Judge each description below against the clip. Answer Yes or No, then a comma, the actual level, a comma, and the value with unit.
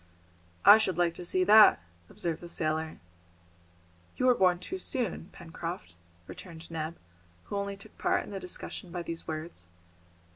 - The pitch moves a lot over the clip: No, average, 3.4 semitones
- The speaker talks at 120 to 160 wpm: Yes, average, 155 wpm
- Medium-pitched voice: Yes, medium, 175 Hz